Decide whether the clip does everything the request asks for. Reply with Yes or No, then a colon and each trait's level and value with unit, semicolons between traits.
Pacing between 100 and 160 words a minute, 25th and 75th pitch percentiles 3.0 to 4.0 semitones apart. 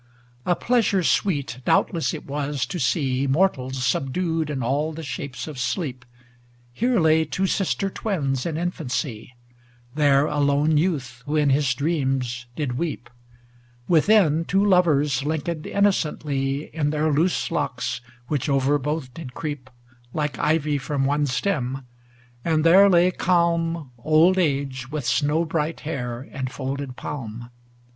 Yes: average, 140 wpm; average, 3.7 semitones